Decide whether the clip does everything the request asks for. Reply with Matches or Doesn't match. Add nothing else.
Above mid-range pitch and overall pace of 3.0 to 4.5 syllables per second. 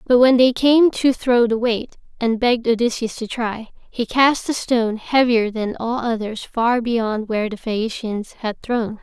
Matches